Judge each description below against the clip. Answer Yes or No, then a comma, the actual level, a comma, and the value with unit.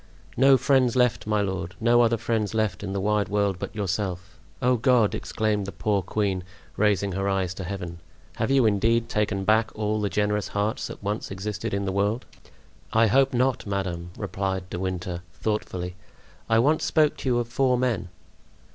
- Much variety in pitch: No, average, 3.2 semitones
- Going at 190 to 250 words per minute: No, average, 180 wpm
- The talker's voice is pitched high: No, low, 105 Hz